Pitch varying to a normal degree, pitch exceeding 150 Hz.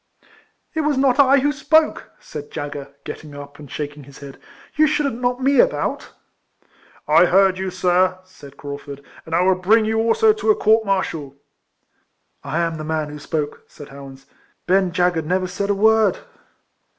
No: wide, 7.2 semitones; medium, 185 Hz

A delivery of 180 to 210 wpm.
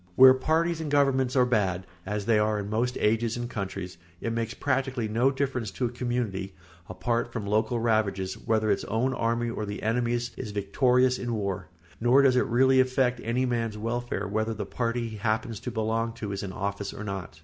Yes: average, 200 wpm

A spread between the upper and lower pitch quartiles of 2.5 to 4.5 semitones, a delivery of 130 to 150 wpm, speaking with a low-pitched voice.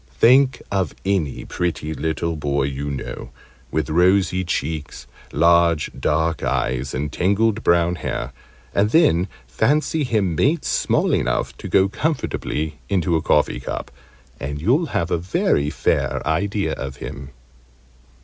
No: average, 5.2 semitones; slow, 135 wpm; very low, 85 Hz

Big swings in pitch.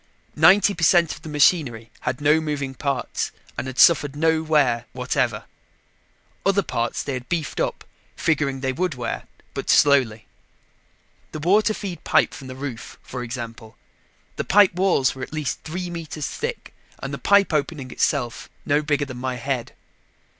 No: average, 4.4 semitones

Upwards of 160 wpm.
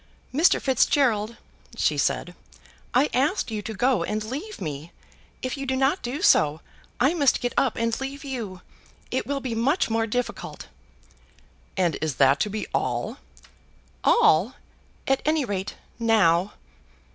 No: average, 145 wpm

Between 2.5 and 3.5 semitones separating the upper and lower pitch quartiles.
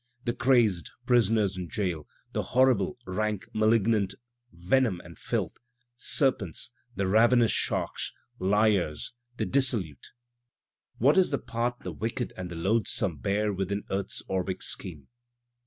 No: average, 4.1 semitones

